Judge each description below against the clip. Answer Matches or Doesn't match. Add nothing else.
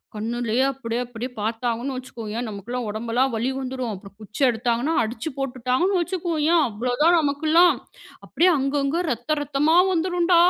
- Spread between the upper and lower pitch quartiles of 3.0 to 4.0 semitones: Doesn't match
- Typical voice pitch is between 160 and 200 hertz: Doesn't match